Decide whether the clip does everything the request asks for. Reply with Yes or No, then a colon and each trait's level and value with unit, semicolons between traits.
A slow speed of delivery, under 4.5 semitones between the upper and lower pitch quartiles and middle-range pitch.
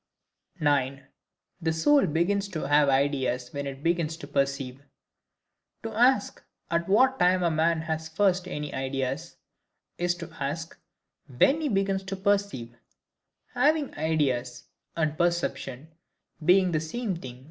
No: slow, 130 wpm; wide, 5.5 semitones; medium, 160 Hz